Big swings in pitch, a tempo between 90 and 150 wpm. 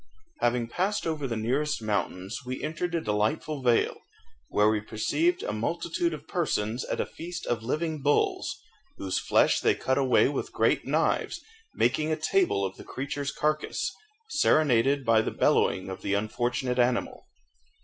No: wide, 5.9 semitones; average, 160 wpm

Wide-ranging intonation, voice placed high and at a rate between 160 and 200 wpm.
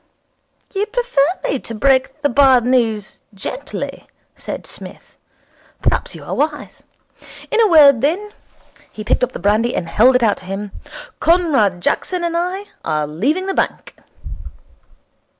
No: wide, 7.8 semitones; very high, 270 Hz; average, 150 wpm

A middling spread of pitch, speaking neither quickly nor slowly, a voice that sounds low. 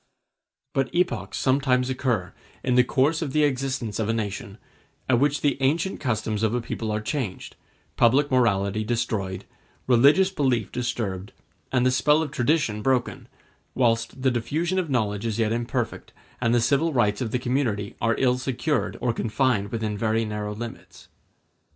Yes: average, 3.6 semitones; average, 165 wpm; low, 120 Hz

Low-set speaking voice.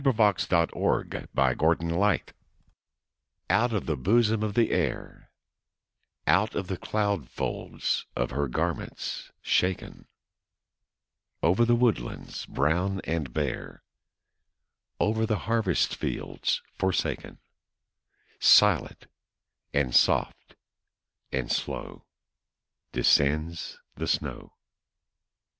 Yes: very low, 90 Hz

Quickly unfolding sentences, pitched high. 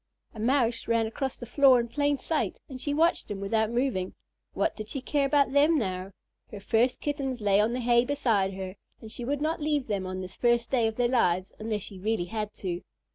Yes: fast, 225 wpm; high, 235 Hz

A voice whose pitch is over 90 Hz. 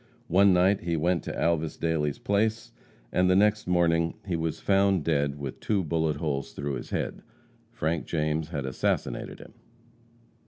No: very low, 85 Hz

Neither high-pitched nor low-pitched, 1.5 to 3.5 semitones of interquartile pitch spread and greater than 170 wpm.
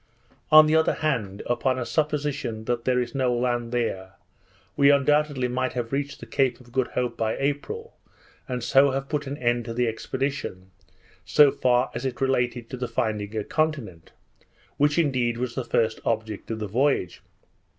No: low, 125 Hz; average, 3.2 semitones; average, 180 wpm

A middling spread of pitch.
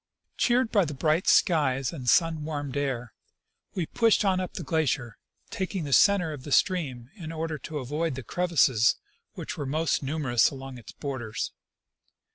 Yes: average, 4.3 semitones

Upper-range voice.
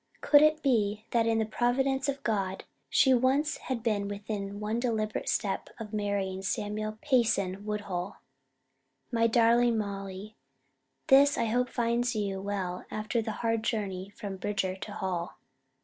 Yes: high, 215 Hz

